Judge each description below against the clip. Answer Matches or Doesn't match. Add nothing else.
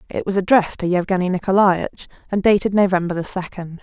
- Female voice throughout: Matches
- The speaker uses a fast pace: Doesn't match